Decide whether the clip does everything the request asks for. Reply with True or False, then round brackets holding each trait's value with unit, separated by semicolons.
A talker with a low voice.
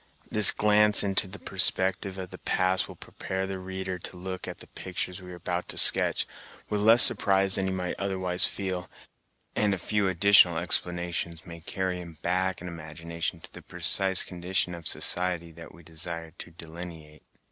True (90 Hz)